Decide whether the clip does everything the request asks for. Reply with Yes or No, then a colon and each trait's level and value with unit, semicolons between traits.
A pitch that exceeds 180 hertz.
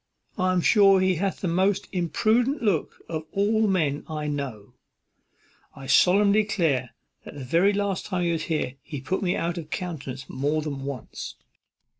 No: medium, 170 Hz